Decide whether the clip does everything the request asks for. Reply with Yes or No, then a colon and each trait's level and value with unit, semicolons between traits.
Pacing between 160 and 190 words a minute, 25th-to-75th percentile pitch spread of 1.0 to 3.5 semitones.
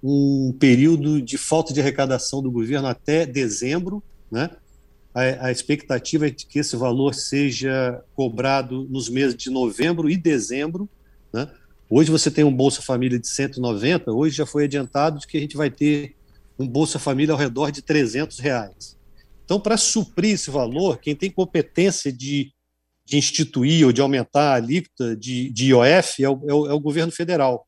Yes: average, 170 wpm; average, 3.1 semitones